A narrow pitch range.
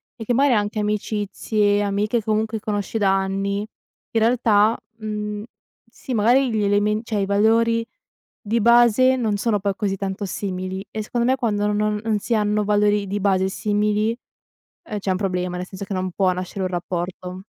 Yes: narrow, 2.0 semitones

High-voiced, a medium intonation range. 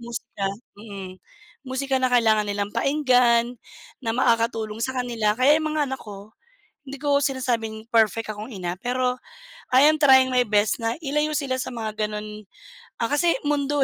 Yes: high, 245 Hz; average, 3.6 semitones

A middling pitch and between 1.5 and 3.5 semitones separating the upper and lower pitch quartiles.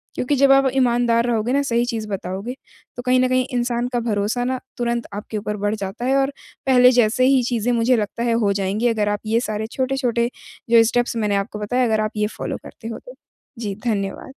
No: high, 235 Hz; average, 2.9 semitones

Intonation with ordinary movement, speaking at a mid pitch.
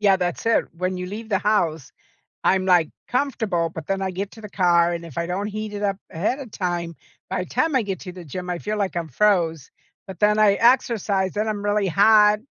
No: average, 3.1 semitones; high, 195 Hz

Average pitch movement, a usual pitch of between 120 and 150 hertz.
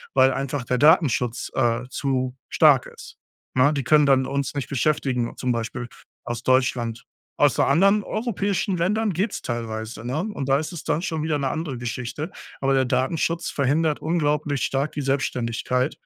Yes: average, 3.8 semitones; low, 135 Hz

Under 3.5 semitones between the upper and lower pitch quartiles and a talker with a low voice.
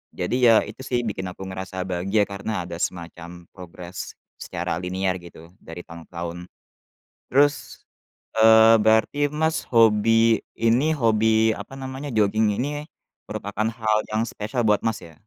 No: average, 3.8 semitones; low, 110 Hz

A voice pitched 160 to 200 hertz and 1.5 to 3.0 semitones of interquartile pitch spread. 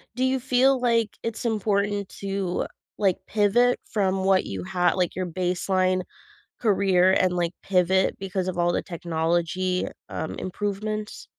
Yes: high, 190 Hz; average, 2.7 semitones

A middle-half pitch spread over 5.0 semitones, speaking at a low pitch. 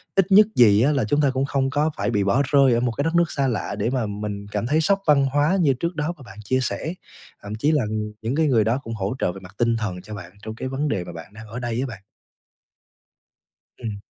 Yes: wide, 5.5 semitones; low, 125 Hz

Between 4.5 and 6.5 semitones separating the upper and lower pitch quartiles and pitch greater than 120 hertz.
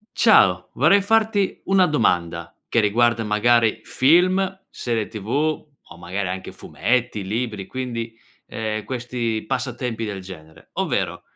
No: average, 5.0 semitones; low, 115 Hz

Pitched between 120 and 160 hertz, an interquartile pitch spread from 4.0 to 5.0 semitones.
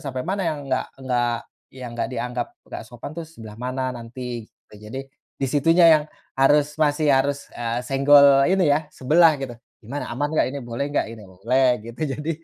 No: low, 135 Hz; average, 3.3 semitones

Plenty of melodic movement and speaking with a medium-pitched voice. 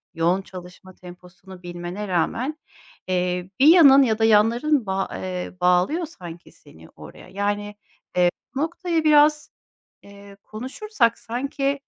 No: wide, 7.5 semitones; high, 205 Hz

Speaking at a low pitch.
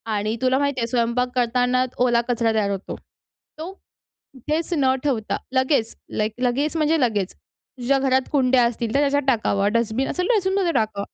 No: very high, 250 Hz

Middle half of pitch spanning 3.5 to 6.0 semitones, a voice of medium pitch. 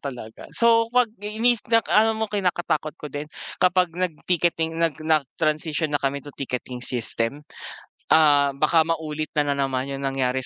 Yes: average, 4.6 semitones; medium, 155 Hz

